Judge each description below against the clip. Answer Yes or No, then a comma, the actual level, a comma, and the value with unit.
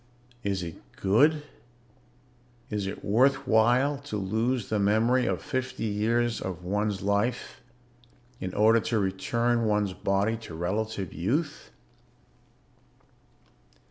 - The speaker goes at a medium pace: No, slow, 110 wpm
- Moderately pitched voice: No, low, 110 Hz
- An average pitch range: Yes, average, 3.4 semitones